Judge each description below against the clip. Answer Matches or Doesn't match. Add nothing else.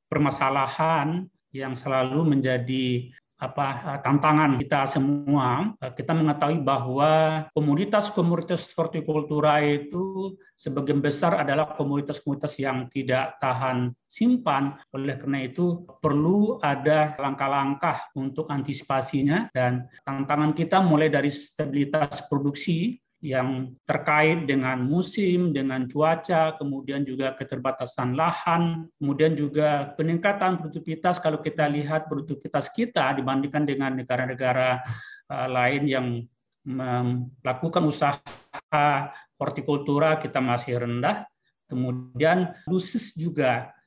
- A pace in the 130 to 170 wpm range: Doesn't match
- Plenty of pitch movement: Doesn't match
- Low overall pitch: Doesn't match